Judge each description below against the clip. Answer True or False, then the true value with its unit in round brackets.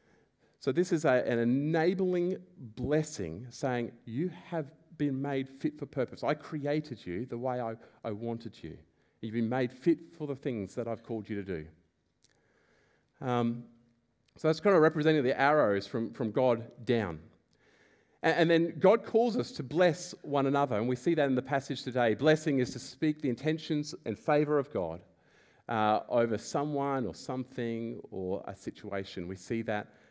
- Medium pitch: False (130 Hz)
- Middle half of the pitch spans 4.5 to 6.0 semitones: True (5.0 semitones)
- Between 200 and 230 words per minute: False (175 wpm)